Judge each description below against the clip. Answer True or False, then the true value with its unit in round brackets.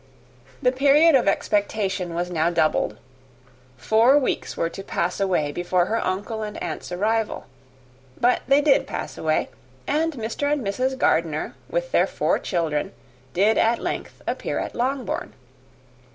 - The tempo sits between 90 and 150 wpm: True (145 wpm)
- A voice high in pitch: True (215 Hz)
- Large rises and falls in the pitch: True (6.8 semitones)